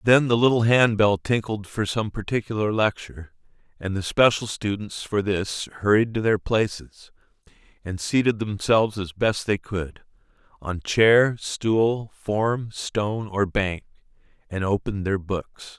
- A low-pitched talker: Yes, low, 105 Hz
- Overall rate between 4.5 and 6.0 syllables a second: No, 4.2 syllables/s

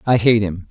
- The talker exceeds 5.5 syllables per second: No, 5.2 syllables/s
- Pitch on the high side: No, low, 105 Hz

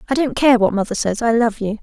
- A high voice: Yes, high, 225 Hz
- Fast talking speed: Yes, fast, 295 wpm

